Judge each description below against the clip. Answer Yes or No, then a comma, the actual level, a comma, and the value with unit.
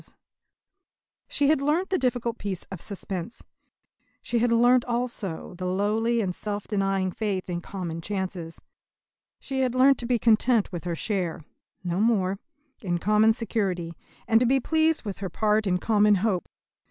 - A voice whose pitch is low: No, high, 210 Hz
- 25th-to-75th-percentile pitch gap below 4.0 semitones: No, average, 4.4 semitones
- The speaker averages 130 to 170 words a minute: Yes, average, 160 wpm